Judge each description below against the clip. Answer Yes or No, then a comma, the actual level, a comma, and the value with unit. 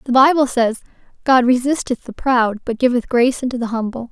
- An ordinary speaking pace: Yes, average, 190 wpm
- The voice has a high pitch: Yes, very high, 250 Hz